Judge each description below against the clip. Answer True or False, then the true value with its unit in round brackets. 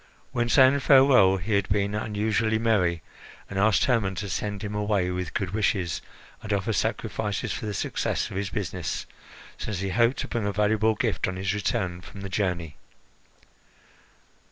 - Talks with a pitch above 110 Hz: False (105 Hz)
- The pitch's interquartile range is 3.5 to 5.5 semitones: False (2.7 semitones)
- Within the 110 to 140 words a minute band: False (170 wpm)